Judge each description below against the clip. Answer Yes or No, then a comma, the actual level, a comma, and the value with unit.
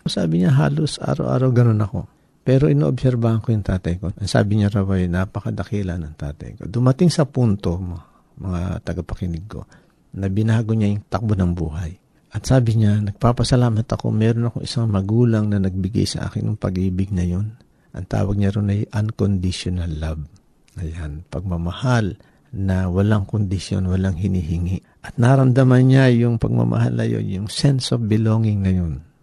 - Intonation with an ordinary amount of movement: Yes, average, 4.4 semitones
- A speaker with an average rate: No, fast, 160 wpm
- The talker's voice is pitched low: Yes, low, 105 Hz